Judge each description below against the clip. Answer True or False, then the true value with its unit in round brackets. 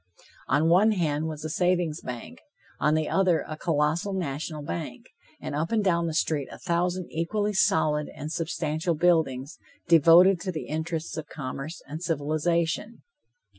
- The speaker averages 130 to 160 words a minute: True (155 wpm)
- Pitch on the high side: False (160 Hz)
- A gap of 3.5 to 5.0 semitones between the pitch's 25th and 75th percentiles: False (2.6 semitones)